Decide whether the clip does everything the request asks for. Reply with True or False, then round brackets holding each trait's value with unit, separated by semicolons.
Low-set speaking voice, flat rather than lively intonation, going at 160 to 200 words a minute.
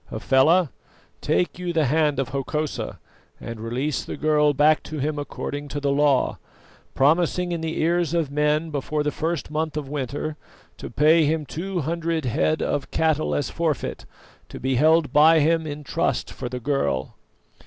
False (150 Hz; 2.3 semitones; 170 wpm)